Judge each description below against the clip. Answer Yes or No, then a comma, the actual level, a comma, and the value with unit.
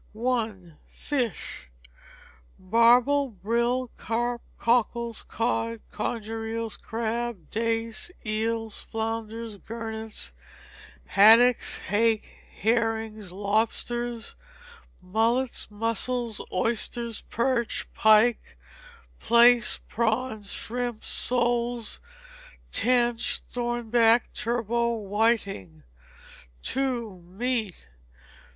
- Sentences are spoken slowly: Yes, slow, 70 wpm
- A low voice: No, high, 230 Hz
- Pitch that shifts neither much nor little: No, narrow, 1.6 semitones